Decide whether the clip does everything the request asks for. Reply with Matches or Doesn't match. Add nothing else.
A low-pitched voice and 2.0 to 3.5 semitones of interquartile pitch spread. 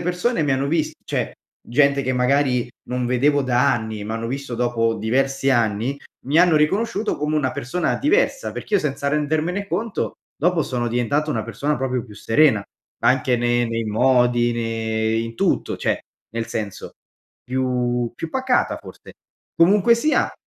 Doesn't match